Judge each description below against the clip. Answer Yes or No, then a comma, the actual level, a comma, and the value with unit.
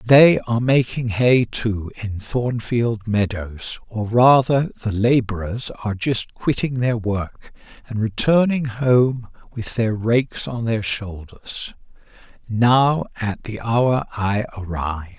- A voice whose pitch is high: No, low, 115 Hz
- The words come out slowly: Yes, slow, 125 wpm